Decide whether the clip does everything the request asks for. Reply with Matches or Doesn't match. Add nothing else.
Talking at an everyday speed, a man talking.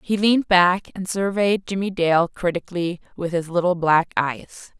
Doesn't match